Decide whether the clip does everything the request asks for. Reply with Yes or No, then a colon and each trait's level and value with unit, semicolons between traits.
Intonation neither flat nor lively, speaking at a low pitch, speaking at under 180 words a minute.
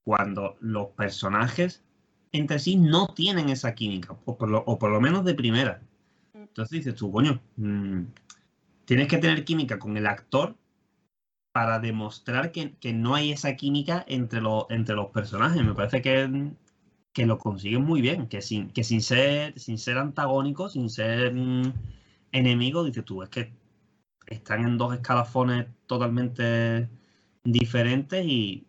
Yes: average, 4.1 semitones; low, 120 Hz; average, 150 wpm